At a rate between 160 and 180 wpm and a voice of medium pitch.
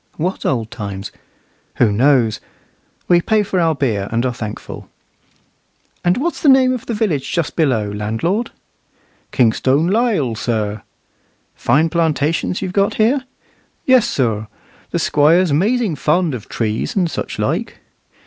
No: average, 140 wpm; medium, 155 Hz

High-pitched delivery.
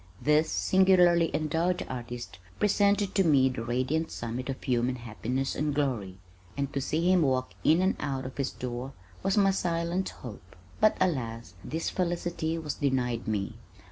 No: medium, 140 Hz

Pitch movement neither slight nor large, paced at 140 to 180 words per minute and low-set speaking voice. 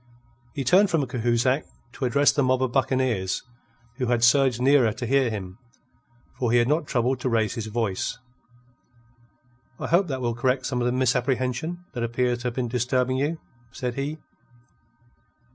No: narrow, 2.1 semitones; average, 170 wpm; low, 125 Hz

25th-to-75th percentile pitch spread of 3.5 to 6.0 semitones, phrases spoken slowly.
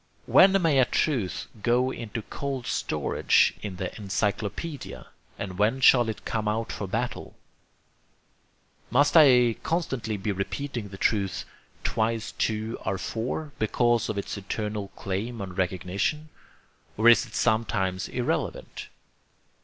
Yes: average, 3.8 semitones; slow, 130 wpm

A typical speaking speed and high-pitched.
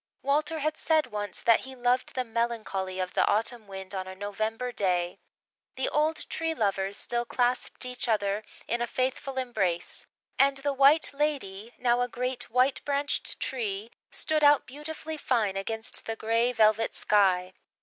Yes: average, 160 wpm; high, 240 Hz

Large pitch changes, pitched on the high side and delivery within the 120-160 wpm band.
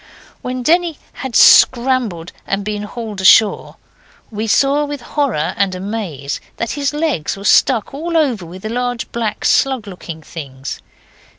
Yes: wide, 5.9 semitones; high, 225 Hz; average, 140 wpm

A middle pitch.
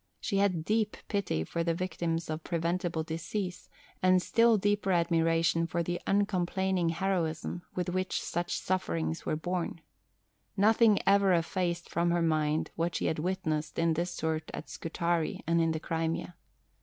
Yes: medium, 170 Hz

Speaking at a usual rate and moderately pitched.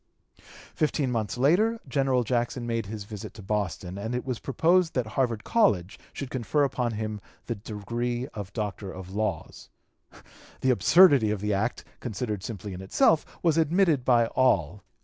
No: average, 160 wpm; low, 115 Hz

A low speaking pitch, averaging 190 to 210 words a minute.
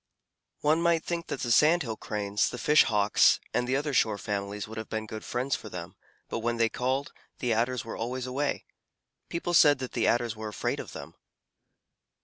Yes: low, 120 Hz; average, 200 wpm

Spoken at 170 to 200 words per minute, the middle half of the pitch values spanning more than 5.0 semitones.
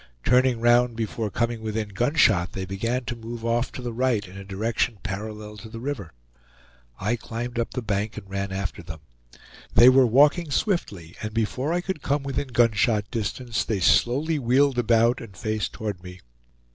No: average, 180 wpm; average, 3.2 semitones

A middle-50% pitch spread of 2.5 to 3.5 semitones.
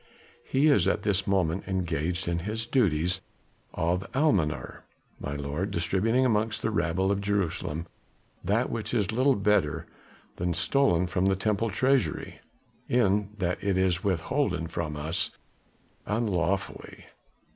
No: average, 4.2 semitones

